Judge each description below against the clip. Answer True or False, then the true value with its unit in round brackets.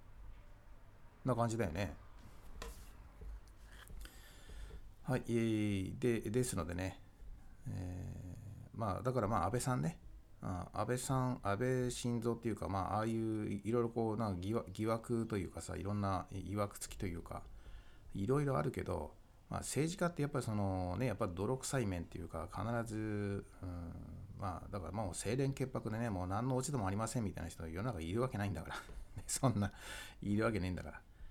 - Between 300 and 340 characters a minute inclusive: True (315 characters per minute)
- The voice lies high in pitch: False (100 Hz)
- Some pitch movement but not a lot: True (4.0 semitones)